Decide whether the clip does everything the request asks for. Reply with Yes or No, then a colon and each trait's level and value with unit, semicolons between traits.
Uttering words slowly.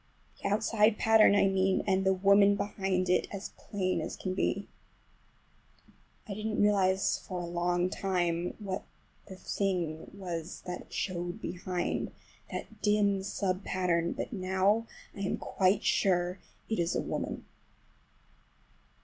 Yes: slow, 130 wpm